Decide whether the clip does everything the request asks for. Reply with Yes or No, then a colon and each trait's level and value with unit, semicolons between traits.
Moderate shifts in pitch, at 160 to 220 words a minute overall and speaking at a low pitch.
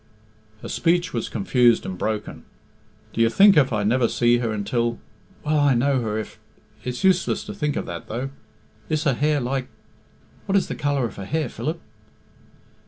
Yes: average, 4.6 semitones; average, 180 wpm; low, 125 Hz